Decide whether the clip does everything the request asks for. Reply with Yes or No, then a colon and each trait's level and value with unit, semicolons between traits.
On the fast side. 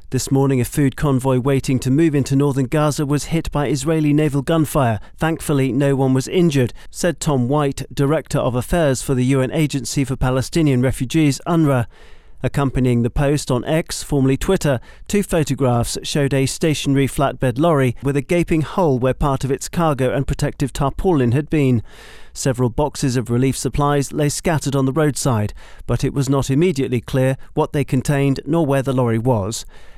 No: average, 175 wpm